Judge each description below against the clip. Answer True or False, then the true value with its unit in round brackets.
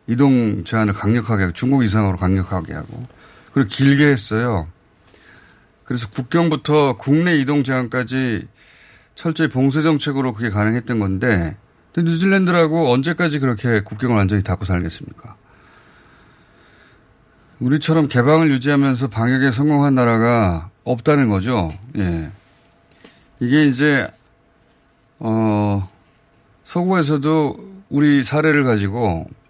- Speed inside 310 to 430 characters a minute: False (275 characters per minute)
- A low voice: True (125 Hz)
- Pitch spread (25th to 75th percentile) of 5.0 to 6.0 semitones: True (5.6 semitones)